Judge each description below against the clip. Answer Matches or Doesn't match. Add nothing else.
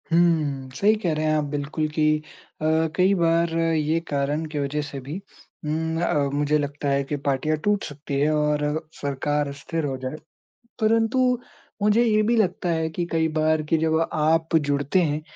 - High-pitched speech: Doesn't match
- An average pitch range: Doesn't match